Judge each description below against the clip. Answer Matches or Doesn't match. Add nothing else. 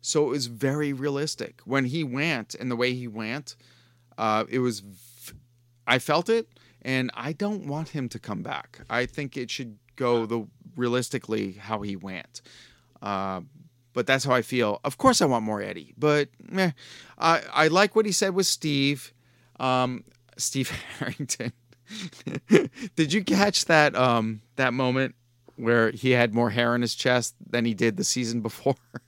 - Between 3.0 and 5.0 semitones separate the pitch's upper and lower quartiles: Matches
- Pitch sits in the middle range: Doesn't match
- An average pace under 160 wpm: Doesn't match